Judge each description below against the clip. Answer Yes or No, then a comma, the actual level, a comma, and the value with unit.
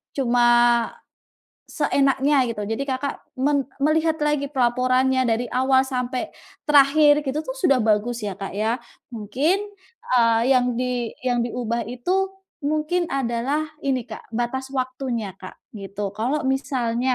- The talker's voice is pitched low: No, very high, 255 Hz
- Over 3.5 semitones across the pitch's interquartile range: No, average, 2.9 semitones